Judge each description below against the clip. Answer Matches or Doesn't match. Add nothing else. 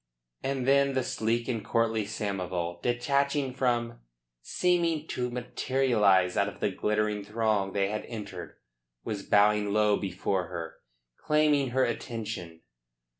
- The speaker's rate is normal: Doesn't match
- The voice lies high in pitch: Doesn't match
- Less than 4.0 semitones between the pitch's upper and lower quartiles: Doesn't match